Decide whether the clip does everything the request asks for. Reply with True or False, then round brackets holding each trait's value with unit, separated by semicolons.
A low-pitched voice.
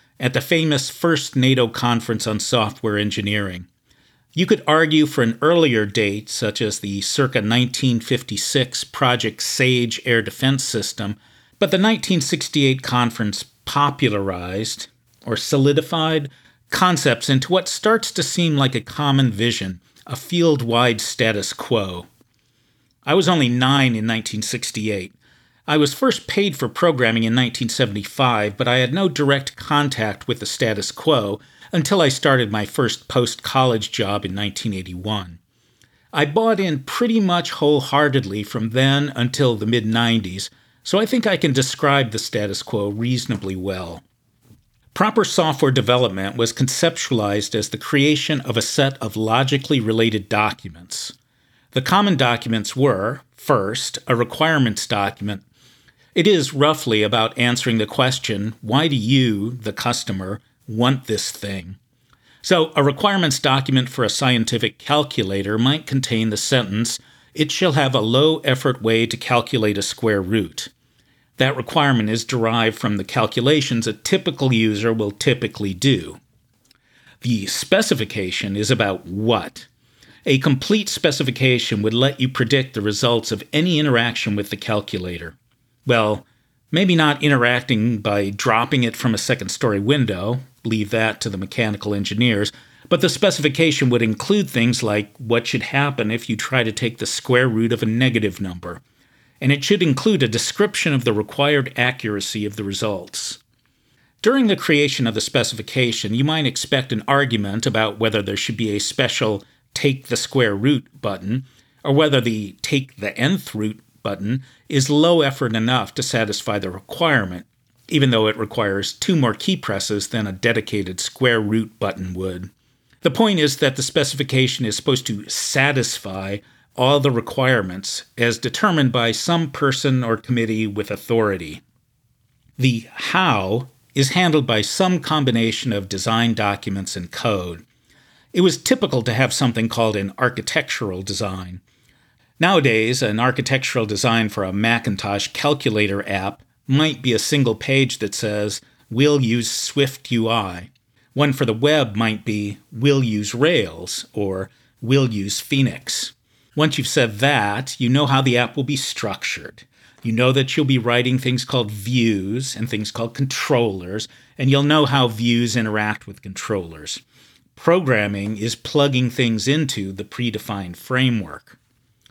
True (120 Hz)